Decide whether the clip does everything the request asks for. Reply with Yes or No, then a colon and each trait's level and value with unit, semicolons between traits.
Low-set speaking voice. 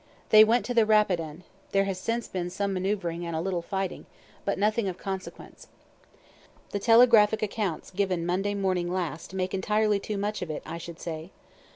No: high, 195 Hz